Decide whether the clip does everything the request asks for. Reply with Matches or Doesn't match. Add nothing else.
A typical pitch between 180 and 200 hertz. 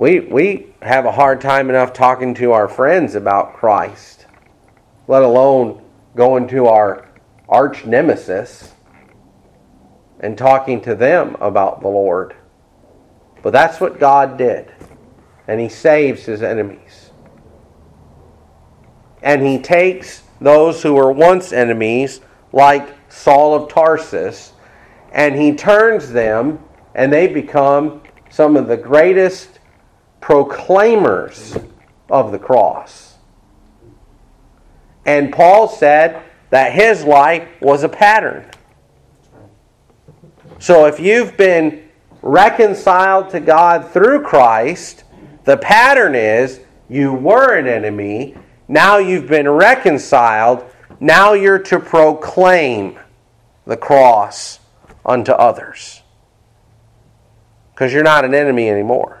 Doesn't match